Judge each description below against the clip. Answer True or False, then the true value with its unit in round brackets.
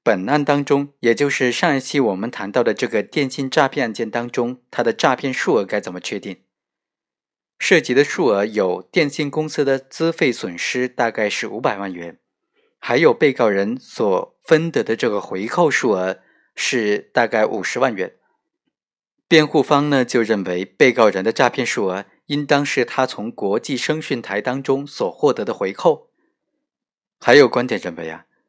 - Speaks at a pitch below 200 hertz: True (140 Hz)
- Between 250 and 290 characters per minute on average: True (255 characters per minute)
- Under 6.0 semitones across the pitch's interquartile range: True (5.6 semitones)